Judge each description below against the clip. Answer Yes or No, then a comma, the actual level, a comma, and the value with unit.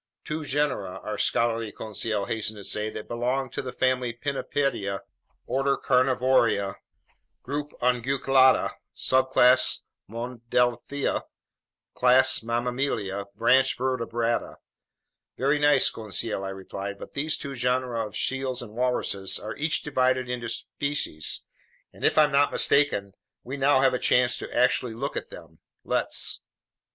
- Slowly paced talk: Yes, slow, 130 wpm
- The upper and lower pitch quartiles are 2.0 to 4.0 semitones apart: Yes, average, 2.9 semitones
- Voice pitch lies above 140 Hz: No, low, 125 Hz